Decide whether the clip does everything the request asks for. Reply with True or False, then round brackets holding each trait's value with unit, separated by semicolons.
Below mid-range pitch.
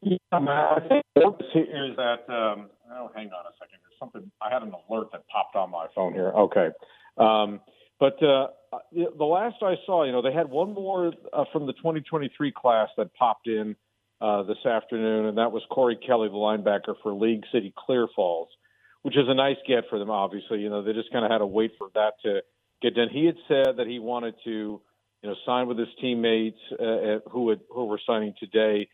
True (115 Hz)